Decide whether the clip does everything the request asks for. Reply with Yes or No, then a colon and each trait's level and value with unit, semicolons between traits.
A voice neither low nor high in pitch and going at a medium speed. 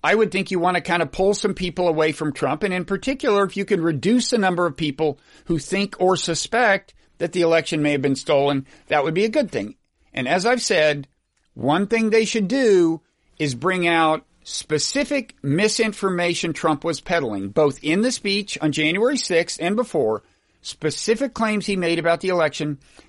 Yes: medium, 175 Hz; average, 195 wpm